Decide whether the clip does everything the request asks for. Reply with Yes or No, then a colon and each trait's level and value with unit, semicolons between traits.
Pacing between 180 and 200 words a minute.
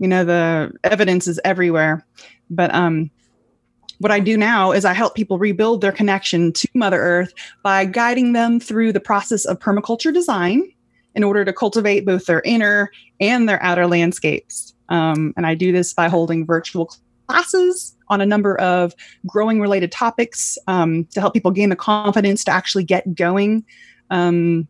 No: average, 170 wpm